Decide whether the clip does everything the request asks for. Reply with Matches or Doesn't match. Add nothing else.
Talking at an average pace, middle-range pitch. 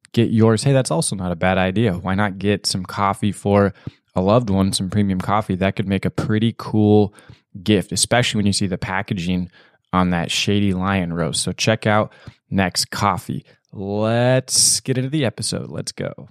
Doesn't match